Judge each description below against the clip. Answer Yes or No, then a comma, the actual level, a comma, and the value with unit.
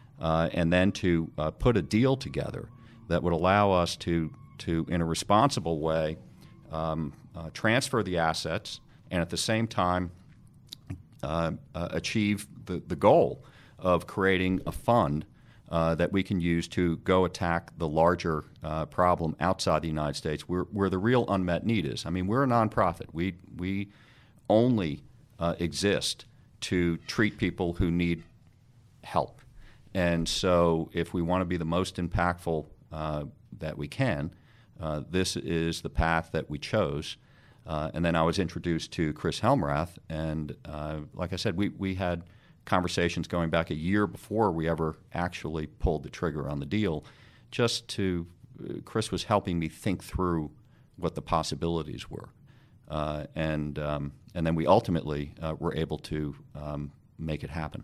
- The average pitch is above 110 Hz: No, very low, 85 Hz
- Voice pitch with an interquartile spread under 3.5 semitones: No, average, 3.9 semitones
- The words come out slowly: No, average, 165 wpm